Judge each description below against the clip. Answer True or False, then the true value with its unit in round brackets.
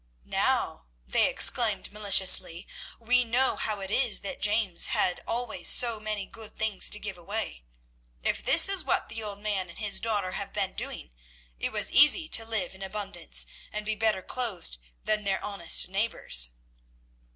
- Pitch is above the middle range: True (210 Hz)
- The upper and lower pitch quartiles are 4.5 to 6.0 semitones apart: False (2.7 semitones)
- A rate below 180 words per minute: True (165 wpm)